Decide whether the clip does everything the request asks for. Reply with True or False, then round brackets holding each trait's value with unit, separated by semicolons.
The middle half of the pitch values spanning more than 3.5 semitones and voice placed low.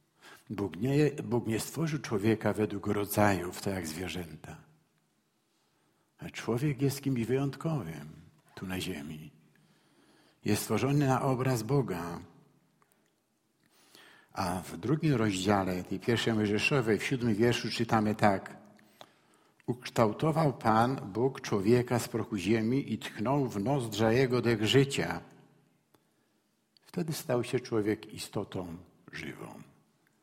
True (4.5 semitones; 115 Hz)